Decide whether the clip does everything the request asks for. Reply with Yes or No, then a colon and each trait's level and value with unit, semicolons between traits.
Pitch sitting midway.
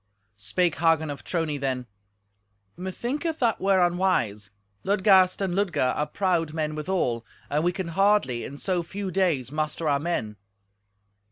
Yes: medium, 170 Hz